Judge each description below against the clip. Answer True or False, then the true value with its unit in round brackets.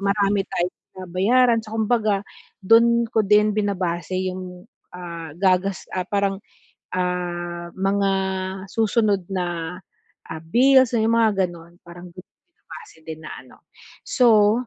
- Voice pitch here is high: True (195 Hz)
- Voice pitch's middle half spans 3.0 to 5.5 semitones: True (3.6 semitones)